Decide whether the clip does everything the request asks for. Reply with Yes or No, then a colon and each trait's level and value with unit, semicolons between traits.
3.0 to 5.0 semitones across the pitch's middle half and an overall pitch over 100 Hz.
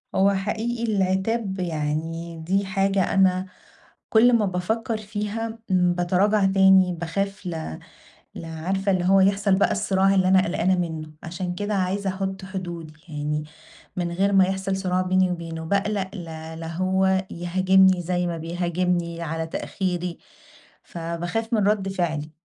No: narrow, 2.4 semitones; medium, 185 Hz